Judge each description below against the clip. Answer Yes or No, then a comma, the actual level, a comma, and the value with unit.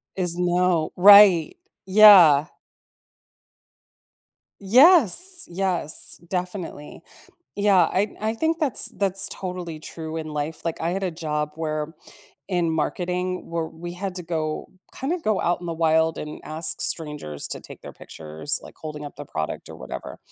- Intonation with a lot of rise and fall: No, average, 3.6 semitones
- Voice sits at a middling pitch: Yes, medium, 175 Hz